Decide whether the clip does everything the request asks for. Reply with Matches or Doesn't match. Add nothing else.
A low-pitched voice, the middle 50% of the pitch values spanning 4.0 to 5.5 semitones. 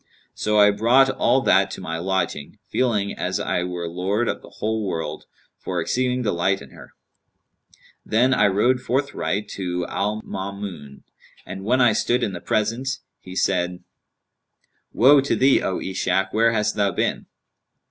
Matches